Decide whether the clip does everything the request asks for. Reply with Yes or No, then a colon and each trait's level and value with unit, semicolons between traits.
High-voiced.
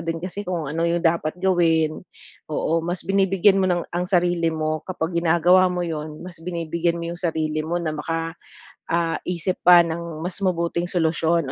No: medium, 170 Hz